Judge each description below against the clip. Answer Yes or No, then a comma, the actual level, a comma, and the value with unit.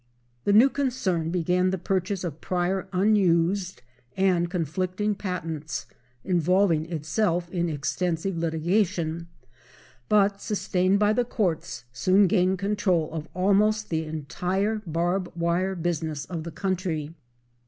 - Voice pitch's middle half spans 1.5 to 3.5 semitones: Yes, average, 2.9 semitones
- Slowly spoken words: Yes, slow, 120 wpm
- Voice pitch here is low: No, medium, 180 Hz